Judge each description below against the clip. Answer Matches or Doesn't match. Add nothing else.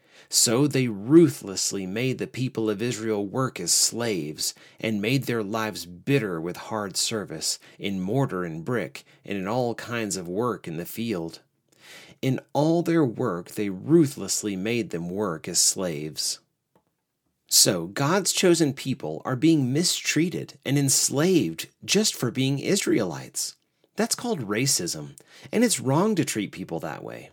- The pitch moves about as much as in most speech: Doesn't match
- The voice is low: Matches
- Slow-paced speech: Doesn't match